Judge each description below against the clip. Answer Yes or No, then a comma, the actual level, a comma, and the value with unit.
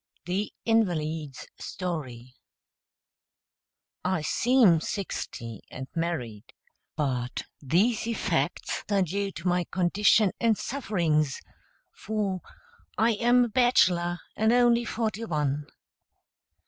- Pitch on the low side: No, medium, 180 Hz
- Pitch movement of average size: No, wide, 6.3 semitones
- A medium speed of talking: No, slow, 95 wpm